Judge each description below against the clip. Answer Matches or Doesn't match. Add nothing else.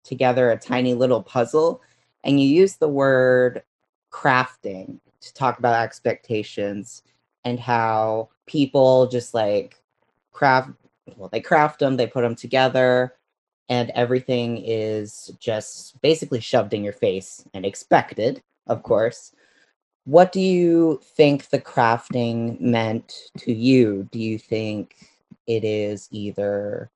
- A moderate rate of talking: Doesn't match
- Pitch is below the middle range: Matches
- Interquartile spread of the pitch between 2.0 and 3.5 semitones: Matches